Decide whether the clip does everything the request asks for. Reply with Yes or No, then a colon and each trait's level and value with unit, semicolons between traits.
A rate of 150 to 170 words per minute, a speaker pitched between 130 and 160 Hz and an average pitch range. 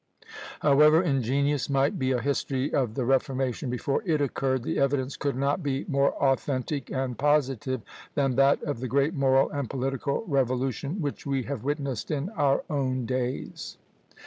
No: average, 160 wpm; low, 135 Hz; narrow, 1.6 semitones